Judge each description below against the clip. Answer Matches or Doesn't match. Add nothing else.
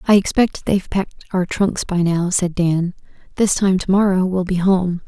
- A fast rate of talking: Doesn't match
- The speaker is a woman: Matches